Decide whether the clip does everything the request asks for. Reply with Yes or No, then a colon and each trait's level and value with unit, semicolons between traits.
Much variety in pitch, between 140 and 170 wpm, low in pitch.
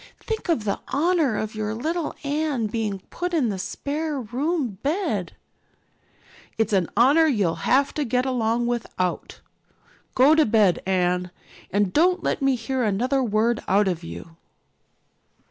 No: wide, 6.0 semitones; average, 145 wpm; high, 240 Hz